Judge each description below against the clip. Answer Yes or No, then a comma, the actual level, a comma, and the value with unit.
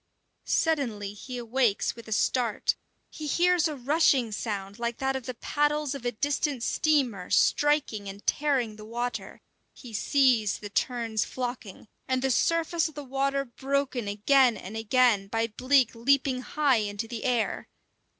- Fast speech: No, average, 155 wpm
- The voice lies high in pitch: Yes, very high, 250 Hz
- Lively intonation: No, average, 4.0 semitones